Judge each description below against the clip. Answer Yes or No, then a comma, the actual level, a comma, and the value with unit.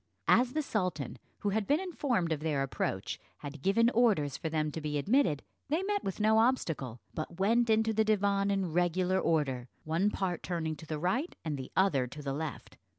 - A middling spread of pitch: No, wide, 6.3 semitones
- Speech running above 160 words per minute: Yes, average, 200 wpm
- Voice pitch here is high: No, medium, 180 Hz